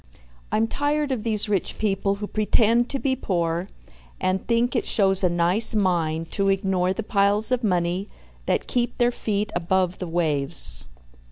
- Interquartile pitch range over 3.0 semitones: Yes, average, 3.9 semitones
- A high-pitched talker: Yes, high, 200 Hz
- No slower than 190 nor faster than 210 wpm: No, average, 165 wpm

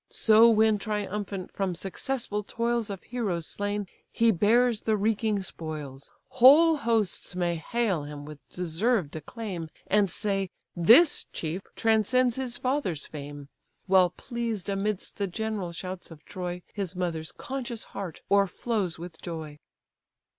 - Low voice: No, high, 200 Hz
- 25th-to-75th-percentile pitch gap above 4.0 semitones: Yes, average, 4.6 semitones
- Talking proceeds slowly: Yes, slow, 130 wpm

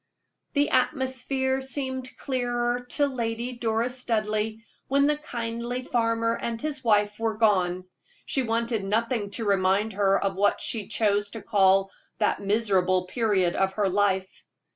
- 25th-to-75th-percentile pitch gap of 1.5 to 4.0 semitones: Yes, average, 3.5 semitones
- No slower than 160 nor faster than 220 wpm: No, average, 140 wpm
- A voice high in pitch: Yes, high, 225 Hz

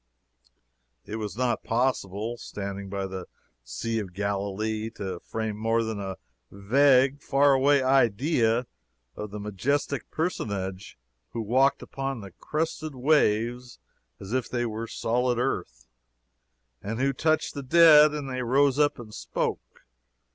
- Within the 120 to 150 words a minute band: Yes, average, 140 wpm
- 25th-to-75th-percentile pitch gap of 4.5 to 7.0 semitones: Yes, average, 4.9 semitones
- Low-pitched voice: Yes, low, 115 Hz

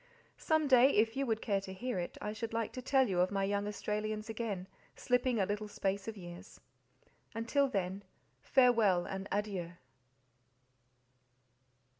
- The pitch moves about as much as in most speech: Yes, average, 3.6 semitones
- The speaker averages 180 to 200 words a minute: No, average, 155 wpm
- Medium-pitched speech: No, high, 210 Hz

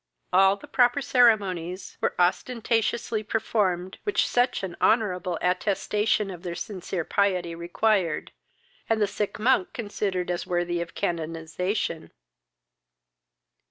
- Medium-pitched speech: No, high, 195 Hz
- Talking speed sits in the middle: No, slow, 115 wpm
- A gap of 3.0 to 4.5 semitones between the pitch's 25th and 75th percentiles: Yes, average, 3.7 semitones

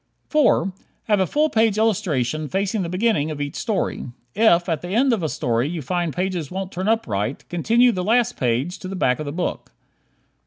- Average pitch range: No, wide, 6.1 semitones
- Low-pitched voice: No, medium, 180 Hz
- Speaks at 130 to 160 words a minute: No, fast, 205 wpm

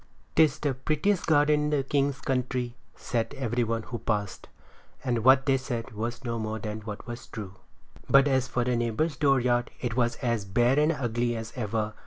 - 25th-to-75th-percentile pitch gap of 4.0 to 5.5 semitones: No, average, 3.0 semitones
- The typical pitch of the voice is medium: No, low, 120 Hz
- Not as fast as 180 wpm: No, average, 190 wpm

